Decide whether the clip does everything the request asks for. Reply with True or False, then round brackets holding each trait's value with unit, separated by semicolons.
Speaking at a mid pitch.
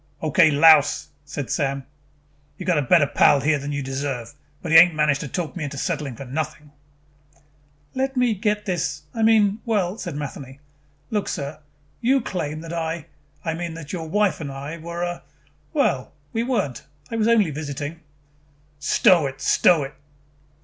True (155 Hz)